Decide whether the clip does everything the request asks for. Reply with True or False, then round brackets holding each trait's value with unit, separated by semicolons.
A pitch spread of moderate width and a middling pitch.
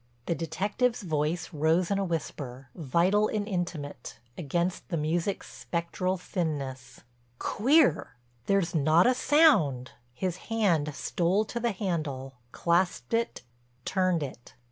True (4.6 semitones; 170 Hz)